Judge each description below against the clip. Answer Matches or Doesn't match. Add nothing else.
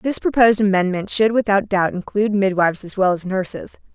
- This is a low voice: Doesn't match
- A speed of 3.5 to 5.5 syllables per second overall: Doesn't match